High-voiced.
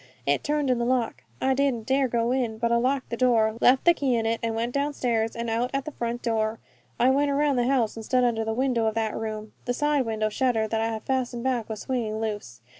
Yes: high, 235 Hz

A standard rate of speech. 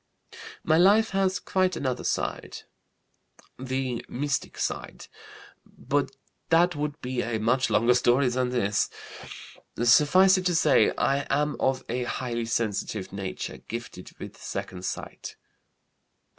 No: slow, 125 wpm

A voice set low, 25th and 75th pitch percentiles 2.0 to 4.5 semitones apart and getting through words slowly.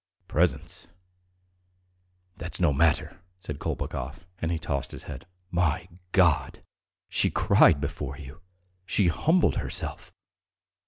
Yes: very low, 80 Hz; average, 3.6 semitones; slow, 110 wpm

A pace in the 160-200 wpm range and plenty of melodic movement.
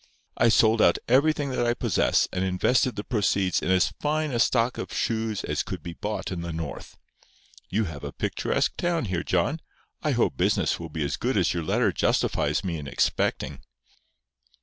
Yes: average, 190 wpm; wide, 6.0 semitones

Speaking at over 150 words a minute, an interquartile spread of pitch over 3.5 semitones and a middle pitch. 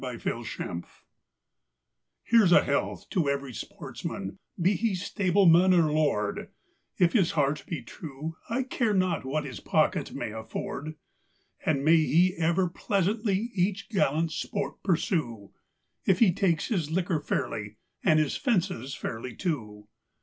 No: average, 140 wpm; wide, 5.4 semitones; medium, 165 Hz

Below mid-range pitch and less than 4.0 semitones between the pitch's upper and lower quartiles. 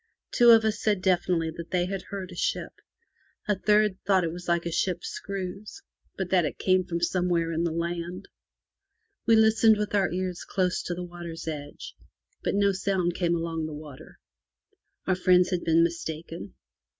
No: medium, 180 Hz; narrow, 2.4 semitones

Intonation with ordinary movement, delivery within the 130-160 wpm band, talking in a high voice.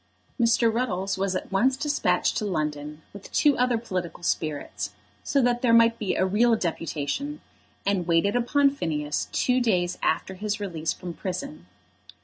No: wide, 5.9 semitones; average, 155 wpm; high, 195 Hz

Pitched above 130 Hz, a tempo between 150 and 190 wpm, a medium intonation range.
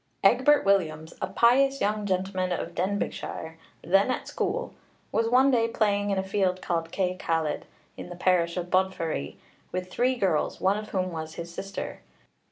Yes: high, 190 Hz; average, 170 wpm; average, 3.7 semitones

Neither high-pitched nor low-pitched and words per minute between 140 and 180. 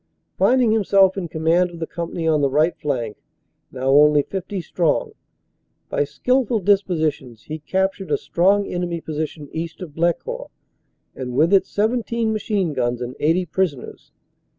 Yes: medium, 170 Hz; average, 150 wpm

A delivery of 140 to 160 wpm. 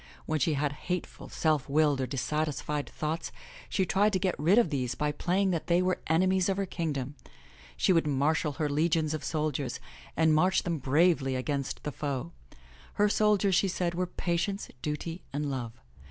No: average, 180 wpm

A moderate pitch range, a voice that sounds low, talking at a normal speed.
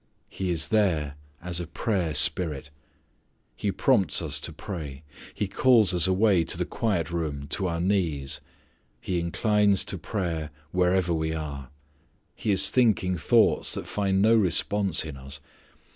Yes: average, 4.2 semitones; very low, 90 Hz; average, 150 wpm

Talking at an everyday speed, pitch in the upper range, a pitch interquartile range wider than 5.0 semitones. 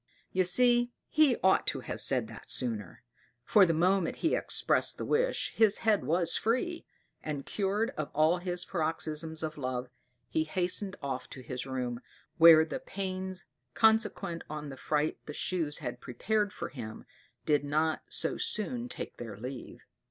No: average, 160 wpm; medium, 165 Hz; wide, 5.6 semitones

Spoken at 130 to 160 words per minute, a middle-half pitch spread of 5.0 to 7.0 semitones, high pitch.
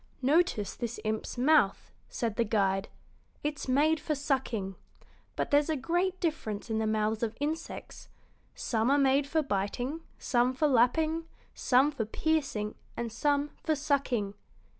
Yes: average, 145 wpm; wide, 5.5 semitones; very high, 265 Hz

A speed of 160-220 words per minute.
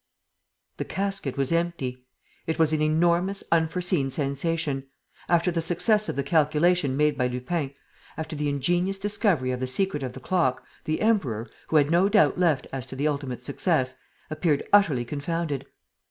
Yes: average, 170 wpm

